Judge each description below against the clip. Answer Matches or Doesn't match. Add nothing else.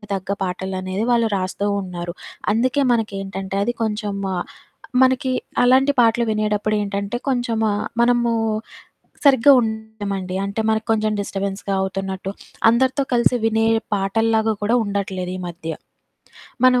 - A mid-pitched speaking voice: Doesn't match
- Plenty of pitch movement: Doesn't match